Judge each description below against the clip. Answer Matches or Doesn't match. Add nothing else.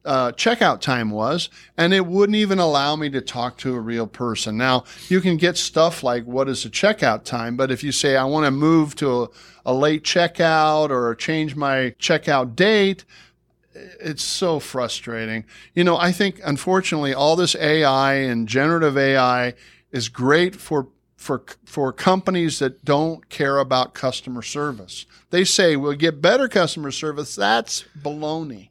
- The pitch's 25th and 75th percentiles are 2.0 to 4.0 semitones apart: Doesn't match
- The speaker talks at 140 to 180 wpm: Matches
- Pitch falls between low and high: Matches